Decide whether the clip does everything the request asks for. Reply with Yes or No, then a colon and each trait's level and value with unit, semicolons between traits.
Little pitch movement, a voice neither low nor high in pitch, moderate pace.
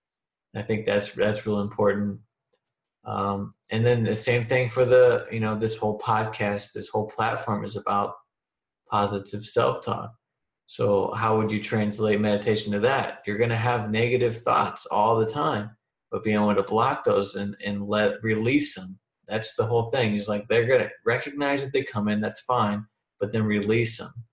No: narrow, 2.2 semitones; low, 110 Hz; average, 180 wpm